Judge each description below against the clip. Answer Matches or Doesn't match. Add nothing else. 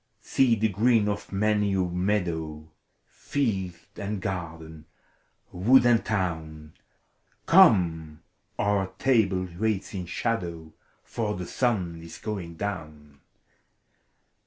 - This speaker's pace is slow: Matches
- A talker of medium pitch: Doesn't match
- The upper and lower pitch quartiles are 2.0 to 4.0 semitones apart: Doesn't match